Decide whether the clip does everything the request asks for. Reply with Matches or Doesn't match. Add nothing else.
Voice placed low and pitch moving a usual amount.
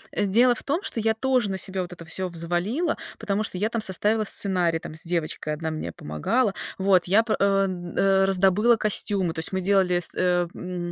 Doesn't match